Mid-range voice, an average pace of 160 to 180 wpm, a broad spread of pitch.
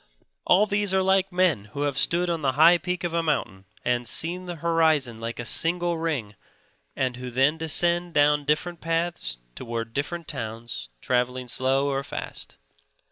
Yes: medium, 150 Hz; average, 170 wpm; wide, 5.7 semitones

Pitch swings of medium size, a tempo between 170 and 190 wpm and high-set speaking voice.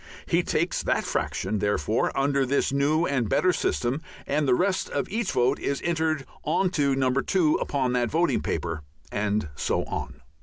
No: average, 4.4 semitones; average, 175 wpm; medium, 140 Hz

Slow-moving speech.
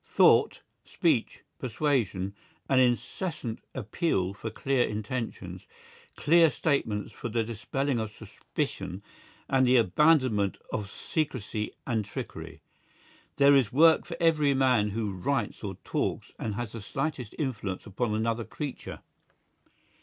Yes: slow, 125 wpm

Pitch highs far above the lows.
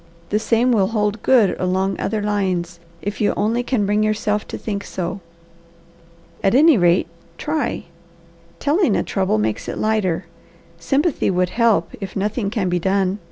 No: average, 3.2 semitones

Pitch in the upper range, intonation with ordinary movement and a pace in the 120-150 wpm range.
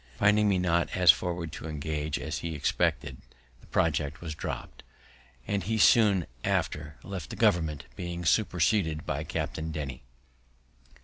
No: very low, 85 Hz; average, 3.4 semitones; average, 140 wpm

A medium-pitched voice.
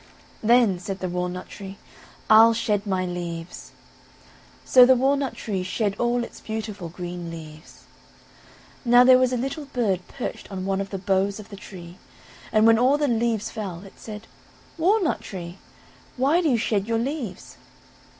No: high, 210 Hz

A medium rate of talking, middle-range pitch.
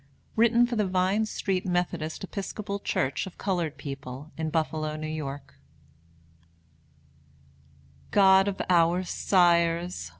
No: slow, 110 wpm; medium, 175 Hz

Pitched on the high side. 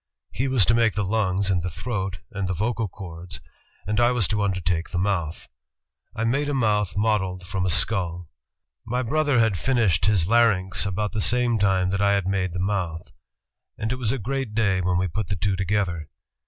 No: low, 100 Hz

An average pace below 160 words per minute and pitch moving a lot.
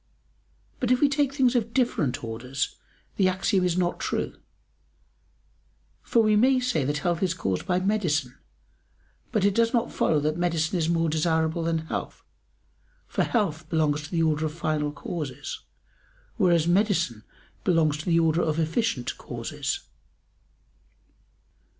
No: average, 145 wpm; average, 4.9 semitones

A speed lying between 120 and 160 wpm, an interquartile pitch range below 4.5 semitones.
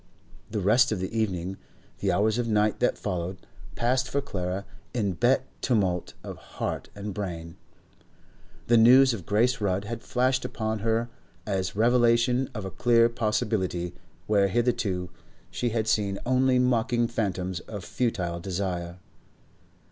Yes: average, 140 wpm; average, 4.1 semitones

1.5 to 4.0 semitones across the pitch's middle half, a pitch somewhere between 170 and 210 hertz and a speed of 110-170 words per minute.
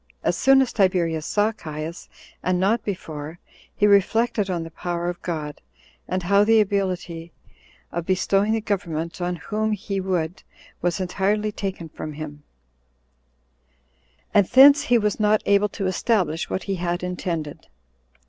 Yes: average, 3.5 semitones; medium, 185 Hz; average, 150 wpm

